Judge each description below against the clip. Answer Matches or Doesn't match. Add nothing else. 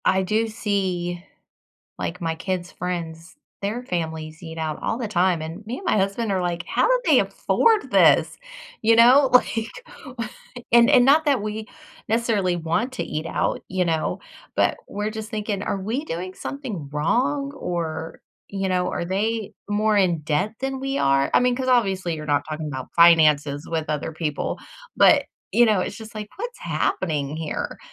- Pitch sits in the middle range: Doesn't match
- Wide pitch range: Matches